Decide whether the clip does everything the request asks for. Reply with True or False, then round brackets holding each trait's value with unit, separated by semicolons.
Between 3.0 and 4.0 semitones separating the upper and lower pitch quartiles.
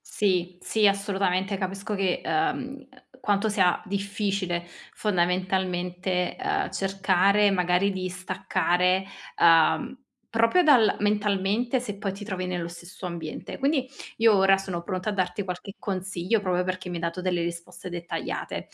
False (2.4 semitones)